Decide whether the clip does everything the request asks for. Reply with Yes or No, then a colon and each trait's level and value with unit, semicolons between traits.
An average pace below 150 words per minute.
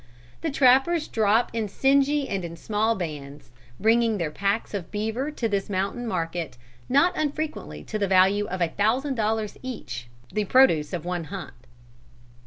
No: average, 160 wpm